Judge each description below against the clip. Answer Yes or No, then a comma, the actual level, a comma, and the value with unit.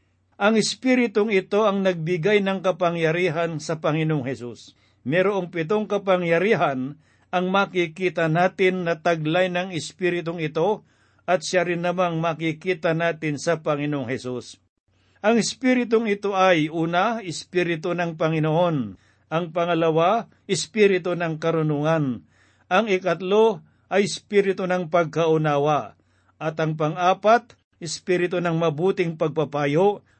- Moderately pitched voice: Yes, medium, 170 Hz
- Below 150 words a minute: Yes, slow, 110 wpm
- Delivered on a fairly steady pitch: No, average, 3.1 semitones